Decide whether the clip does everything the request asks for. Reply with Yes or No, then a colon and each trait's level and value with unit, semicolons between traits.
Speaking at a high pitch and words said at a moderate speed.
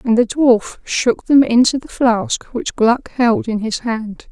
Yes: high, 240 Hz; average, 195 wpm